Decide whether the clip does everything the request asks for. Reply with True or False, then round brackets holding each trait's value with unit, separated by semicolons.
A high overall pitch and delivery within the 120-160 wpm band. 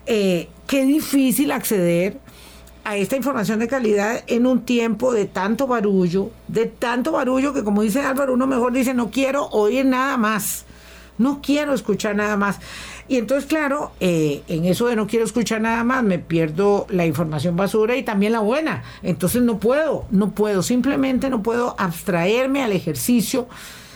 False (225 Hz; 170 wpm)